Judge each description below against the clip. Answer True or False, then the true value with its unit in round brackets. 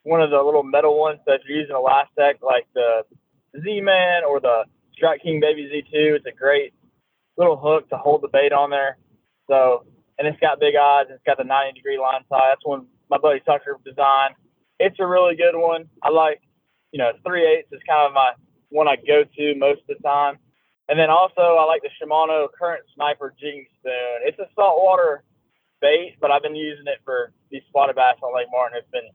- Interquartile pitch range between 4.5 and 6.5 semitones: False (2.8 semitones)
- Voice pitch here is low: False (145 Hz)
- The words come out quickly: True (210 wpm)